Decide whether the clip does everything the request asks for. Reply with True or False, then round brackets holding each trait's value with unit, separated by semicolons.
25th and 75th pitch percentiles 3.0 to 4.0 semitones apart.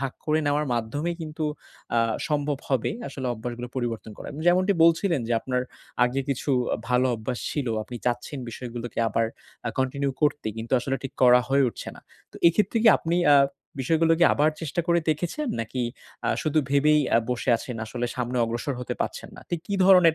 False (4.4 semitones)